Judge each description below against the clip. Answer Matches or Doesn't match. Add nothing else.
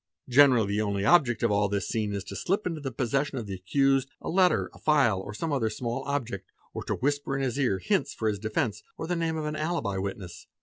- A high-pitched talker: Doesn't match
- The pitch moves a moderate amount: Doesn't match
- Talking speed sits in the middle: Doesn't match